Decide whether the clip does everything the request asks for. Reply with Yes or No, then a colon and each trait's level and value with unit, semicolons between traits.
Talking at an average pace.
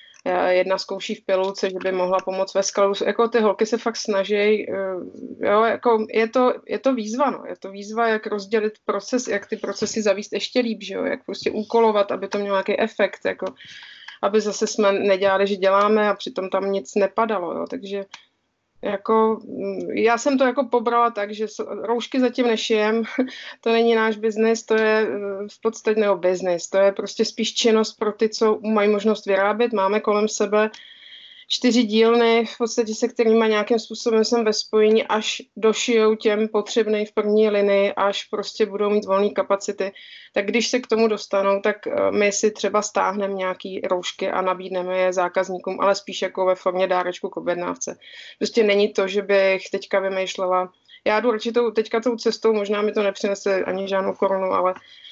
No: fast, 180 wpm